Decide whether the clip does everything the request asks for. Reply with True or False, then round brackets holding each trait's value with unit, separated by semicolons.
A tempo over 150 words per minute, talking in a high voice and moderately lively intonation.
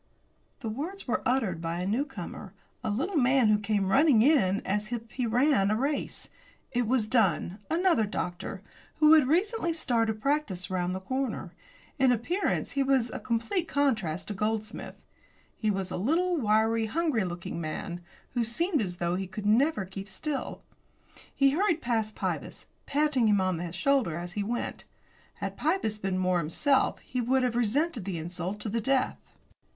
False (170 wpm; 225 Hz; 6.1 semitones)